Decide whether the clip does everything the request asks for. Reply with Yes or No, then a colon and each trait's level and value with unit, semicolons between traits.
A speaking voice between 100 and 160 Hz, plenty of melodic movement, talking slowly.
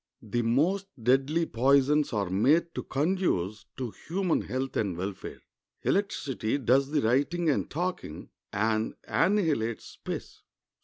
Yes: low, 135 Hz; wide, 6.8 semitones; slow, 120 wpm